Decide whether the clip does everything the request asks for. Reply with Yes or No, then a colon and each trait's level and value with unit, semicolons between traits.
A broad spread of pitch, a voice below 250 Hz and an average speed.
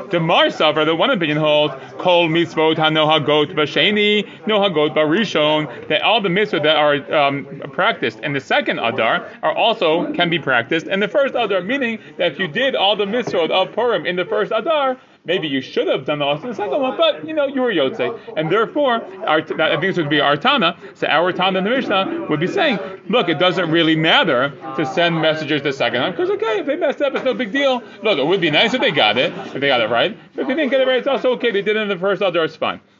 No: wide, 7.9 semitones; high, 190 Hz; fast, 255 wpm